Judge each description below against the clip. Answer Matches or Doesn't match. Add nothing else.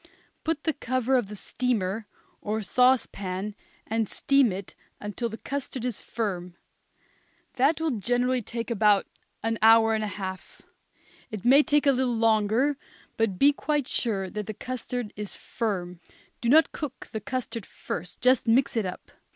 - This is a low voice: Doesn't match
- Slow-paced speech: Doesn't match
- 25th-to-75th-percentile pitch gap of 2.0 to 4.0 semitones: Matches